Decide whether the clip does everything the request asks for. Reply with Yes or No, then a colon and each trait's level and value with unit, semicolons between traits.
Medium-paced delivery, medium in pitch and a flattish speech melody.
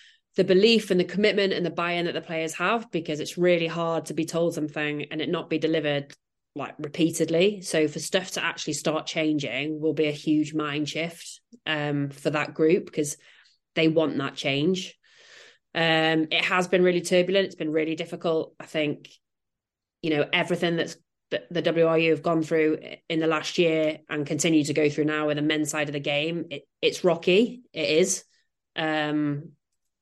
Yes: average, 190 wpm; medium, 160 Hz; narrow, 2.3 semitones